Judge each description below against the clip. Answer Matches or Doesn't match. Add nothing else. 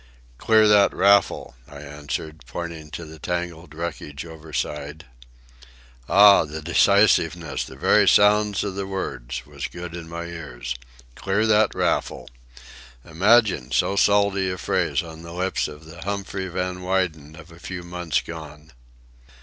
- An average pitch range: Matches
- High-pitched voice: Doesn't match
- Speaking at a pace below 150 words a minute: Matches